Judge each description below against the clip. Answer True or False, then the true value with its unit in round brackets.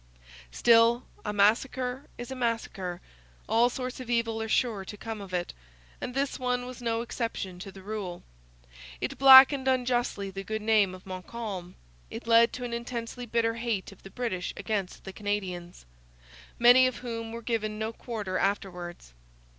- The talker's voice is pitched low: False (225 Hz)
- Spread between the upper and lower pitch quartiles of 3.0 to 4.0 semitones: True (3.7 semitones)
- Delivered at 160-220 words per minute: True (165 wpm)